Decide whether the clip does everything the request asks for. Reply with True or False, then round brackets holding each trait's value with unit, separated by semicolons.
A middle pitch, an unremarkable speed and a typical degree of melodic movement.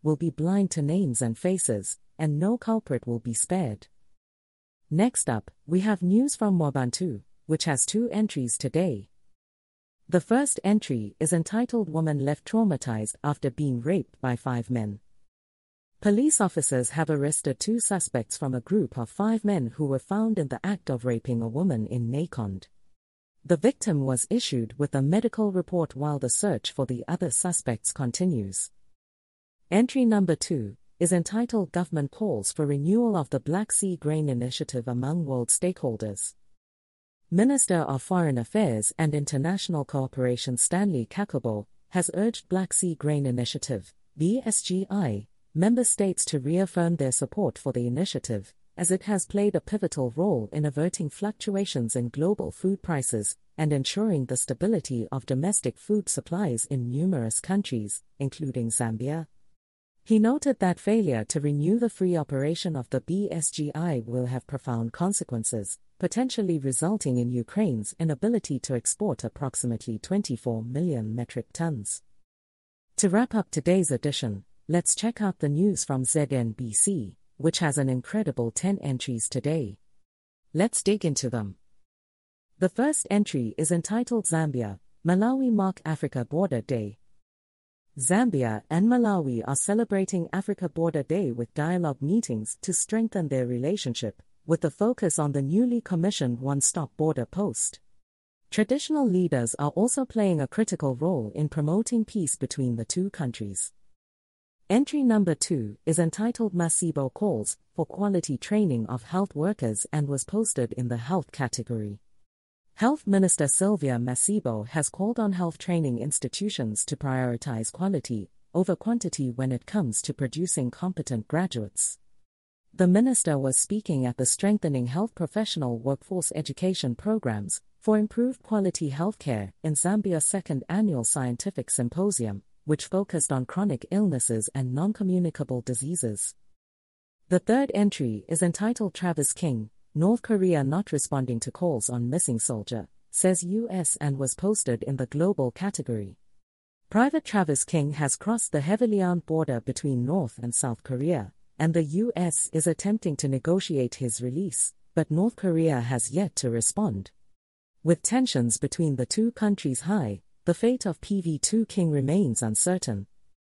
False (150 Hz; 145 wpm; 7.7 semitones)